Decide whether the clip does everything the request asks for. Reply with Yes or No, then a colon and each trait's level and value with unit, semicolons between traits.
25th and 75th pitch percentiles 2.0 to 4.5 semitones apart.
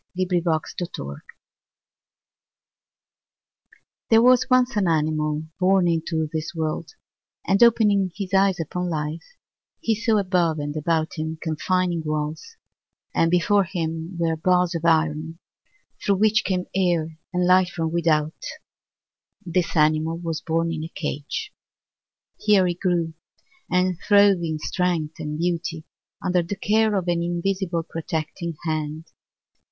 Yes: average, 2.7 semitones